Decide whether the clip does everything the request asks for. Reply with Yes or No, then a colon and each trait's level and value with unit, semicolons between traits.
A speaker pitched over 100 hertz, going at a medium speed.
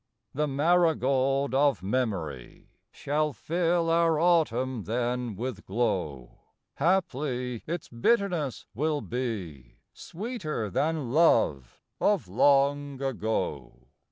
No: low, 135 Hz; slow, 95 wpm